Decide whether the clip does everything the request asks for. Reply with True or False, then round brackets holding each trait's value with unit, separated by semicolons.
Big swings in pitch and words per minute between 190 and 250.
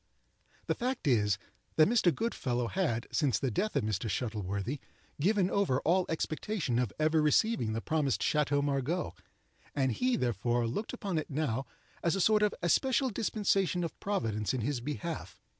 False (8.2 semitones; 160 wpm)